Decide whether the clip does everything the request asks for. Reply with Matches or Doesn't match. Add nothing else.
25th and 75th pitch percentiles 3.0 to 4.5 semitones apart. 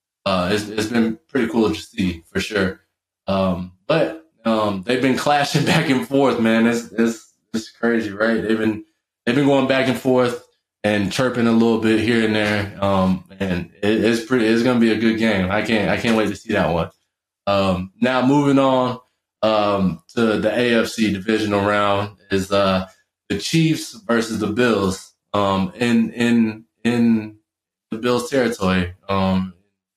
Matches